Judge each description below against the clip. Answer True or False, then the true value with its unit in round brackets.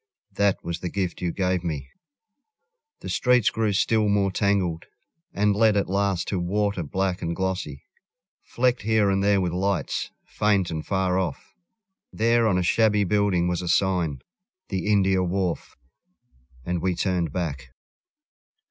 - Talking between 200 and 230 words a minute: False (155 wpm)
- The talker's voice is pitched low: True (95 Hz)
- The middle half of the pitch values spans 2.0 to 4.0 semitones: True (2.7 semitones)